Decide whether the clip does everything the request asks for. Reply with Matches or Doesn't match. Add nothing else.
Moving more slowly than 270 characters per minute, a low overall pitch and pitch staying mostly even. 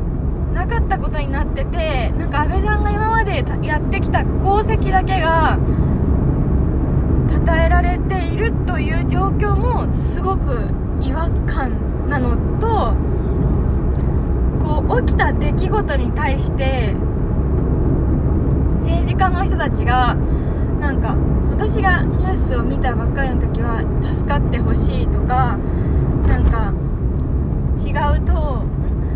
Matches